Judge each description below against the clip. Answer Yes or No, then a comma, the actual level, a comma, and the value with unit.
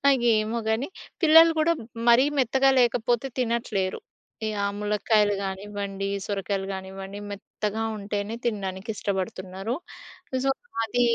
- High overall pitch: Yes, high, 210 Hz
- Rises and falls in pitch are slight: No, average, 3.4 semitones